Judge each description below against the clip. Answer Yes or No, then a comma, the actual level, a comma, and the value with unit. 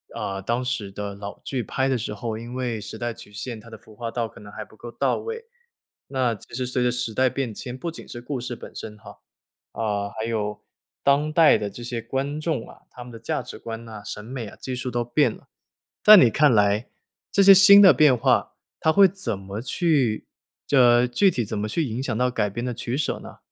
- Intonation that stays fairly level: No, average, 3.4 semitones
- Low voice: Yes, low, 120 Hz